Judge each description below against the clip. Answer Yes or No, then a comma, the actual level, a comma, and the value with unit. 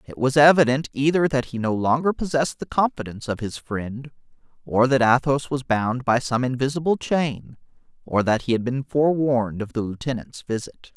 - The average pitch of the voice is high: No, low, 130 Hz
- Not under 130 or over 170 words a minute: No, average, 180 wpm